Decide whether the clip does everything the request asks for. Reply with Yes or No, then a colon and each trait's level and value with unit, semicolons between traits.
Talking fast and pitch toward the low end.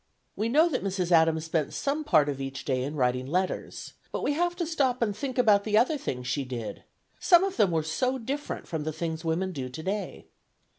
No: fast, 215 wpm; medium, 185 Hz